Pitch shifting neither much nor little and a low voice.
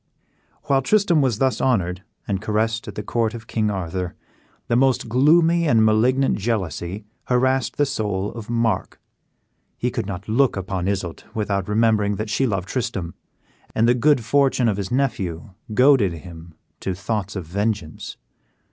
Yes: average, 4.5 semitones; low, 110 Hz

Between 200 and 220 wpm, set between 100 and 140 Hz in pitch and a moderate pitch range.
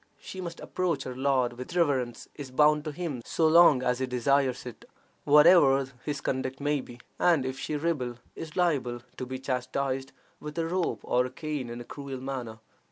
No: average, 190 wpm; low, 135 Hz; average, 3.1 semitones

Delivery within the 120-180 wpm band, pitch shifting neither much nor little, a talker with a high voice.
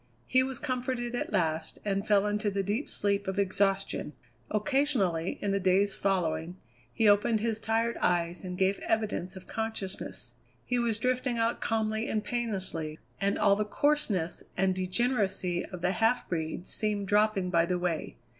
Yes: average, 165 wpm; average, 3.4 semitones; high, 200 Hz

